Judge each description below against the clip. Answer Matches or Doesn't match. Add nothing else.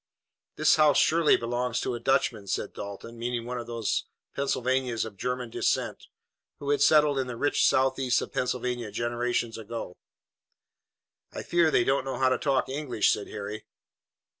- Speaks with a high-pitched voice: Doesn't match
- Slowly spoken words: Doesn't match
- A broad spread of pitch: Doesn't match